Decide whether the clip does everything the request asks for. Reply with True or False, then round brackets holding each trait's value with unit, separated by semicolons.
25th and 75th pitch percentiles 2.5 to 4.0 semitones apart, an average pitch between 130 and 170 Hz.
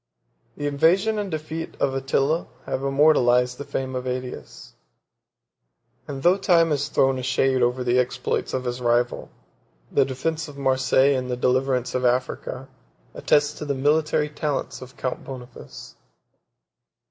True (2.9 semitones; 135 Hz)